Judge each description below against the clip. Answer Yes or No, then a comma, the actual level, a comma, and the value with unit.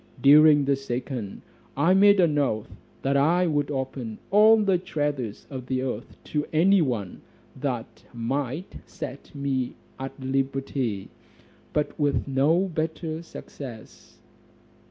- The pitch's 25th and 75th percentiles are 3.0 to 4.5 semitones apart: Yes, average, 3.4 semitones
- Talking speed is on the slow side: Yes, slow, 125 wpm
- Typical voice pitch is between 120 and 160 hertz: Yes, medium, 140 Hz